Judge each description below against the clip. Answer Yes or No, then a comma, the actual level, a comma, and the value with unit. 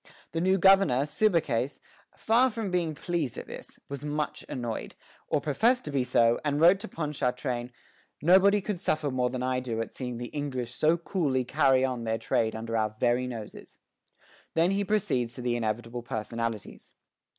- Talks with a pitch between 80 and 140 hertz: Yes, low, 135 Hz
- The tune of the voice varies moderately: No, wide, 6.0 semitones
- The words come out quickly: No, average, 175 wpm